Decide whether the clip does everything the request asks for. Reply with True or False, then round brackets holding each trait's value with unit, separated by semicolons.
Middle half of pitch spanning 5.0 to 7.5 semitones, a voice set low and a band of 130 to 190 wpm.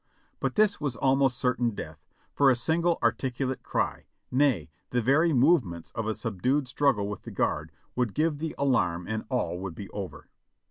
True (5.5 semitones; 125 Hz; 175 wpm)